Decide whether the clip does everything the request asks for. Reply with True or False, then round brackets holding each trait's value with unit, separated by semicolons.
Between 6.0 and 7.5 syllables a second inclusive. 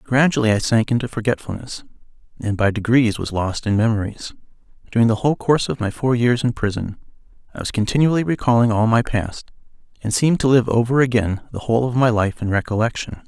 True (6.2 syllables/s)